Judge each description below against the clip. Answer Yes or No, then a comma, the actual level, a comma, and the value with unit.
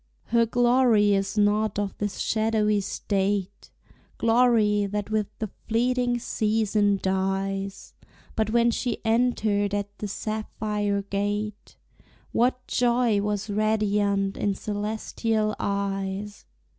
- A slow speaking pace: Yes, slow, 105 wpm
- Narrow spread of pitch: Yes, narrow, 1.8 semitones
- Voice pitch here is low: No, high, 210 Hz